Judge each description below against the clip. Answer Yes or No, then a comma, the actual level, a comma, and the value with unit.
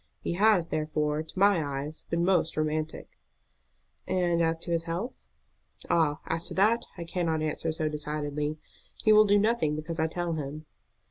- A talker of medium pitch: Yes, medium, 165 Hz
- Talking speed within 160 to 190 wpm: Yes, average, 165 wpm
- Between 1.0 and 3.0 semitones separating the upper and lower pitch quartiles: Yes, narrow, 2.5 semitones